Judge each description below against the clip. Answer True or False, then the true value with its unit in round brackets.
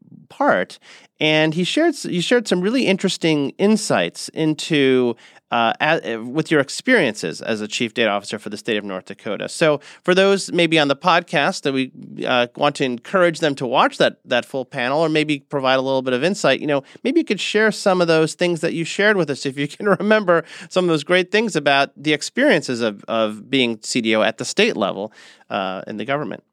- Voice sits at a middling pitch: True (155 Hz)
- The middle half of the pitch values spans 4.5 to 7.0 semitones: True (5.6 semitones)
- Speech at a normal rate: False (215 wpm)